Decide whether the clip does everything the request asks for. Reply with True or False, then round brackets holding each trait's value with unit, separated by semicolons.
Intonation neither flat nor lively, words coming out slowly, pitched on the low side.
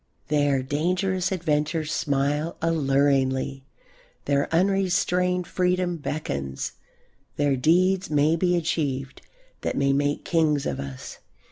False (4.3 semitones; 105 wpm; 150 Hz)